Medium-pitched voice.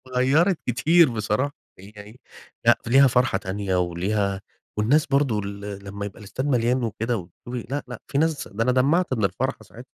No: low, 115 Hz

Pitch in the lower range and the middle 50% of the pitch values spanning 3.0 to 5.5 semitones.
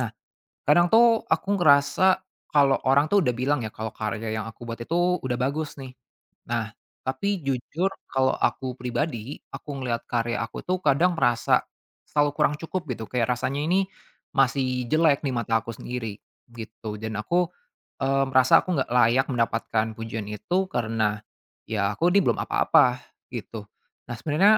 Yes: low, 130 Hz; average, 4.1 semitones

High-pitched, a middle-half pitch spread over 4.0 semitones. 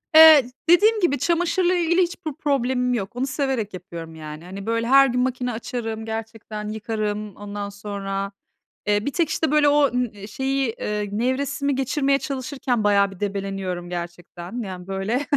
Yes: high, 230 Hz; wide, 5.4 semitones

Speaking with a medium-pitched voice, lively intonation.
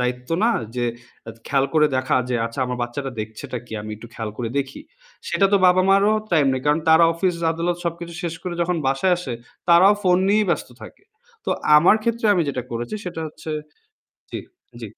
Yes: medium, 160 Hz; wide, 6.0 semitones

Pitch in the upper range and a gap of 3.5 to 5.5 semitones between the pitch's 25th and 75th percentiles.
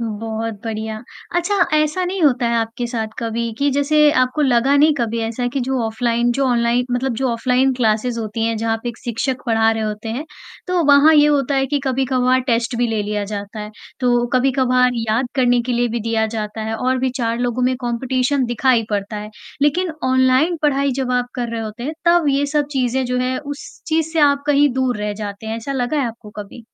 No: high, 245 Hz; average, 3.1 semitones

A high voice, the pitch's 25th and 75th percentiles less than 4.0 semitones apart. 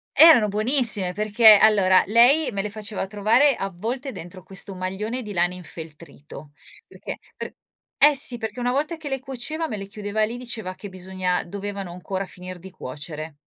No: high, 205 Hz; average, 4.6 semitones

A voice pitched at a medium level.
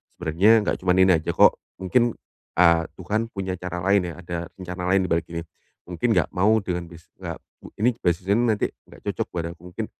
No: very low, 90 Hz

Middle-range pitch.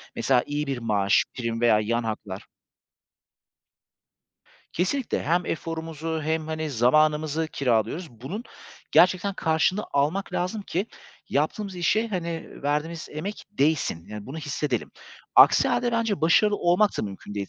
Yes: medium, 155 Hz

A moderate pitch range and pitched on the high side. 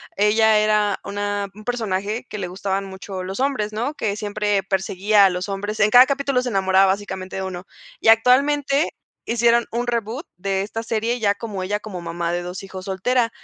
Yes: average, 3.2 semitones; high, 205 Hz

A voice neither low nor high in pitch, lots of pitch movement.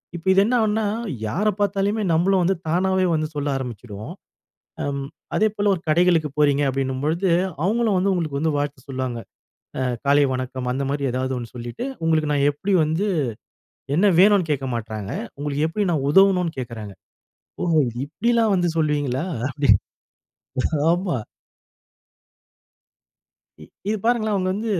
Yes: medium, 155 Hz; wide, 6.2 semitones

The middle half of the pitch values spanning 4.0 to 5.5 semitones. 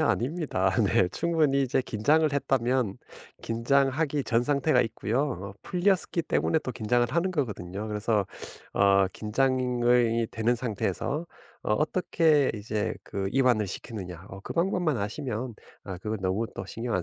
Yes: average, 5.2 semitones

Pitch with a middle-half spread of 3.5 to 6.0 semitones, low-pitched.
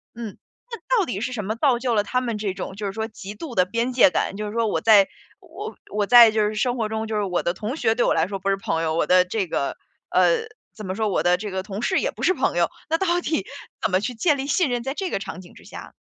No: average, 4.3 semitones; high, 220 Hz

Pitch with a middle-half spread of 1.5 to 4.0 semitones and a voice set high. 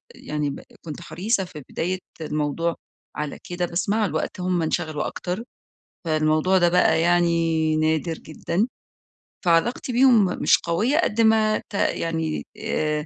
No: average, 3.4 semitones; medium, 170 Hz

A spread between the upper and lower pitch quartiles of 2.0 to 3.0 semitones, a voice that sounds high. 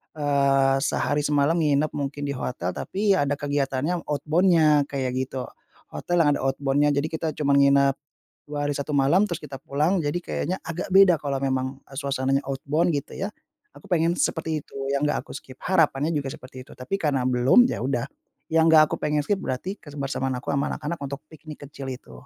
No: average, 2.7 semitones; medium, 145 Hz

